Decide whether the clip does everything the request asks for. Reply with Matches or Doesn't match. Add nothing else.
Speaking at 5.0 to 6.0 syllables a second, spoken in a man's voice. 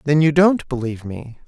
Matches